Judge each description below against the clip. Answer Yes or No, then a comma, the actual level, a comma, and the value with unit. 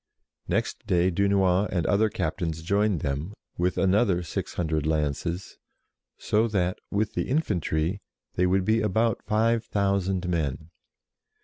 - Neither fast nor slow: No, slow, 130 wpm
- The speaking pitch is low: Yes, very low, 95 Hz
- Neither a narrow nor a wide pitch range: Yes, average, 3.7 semitones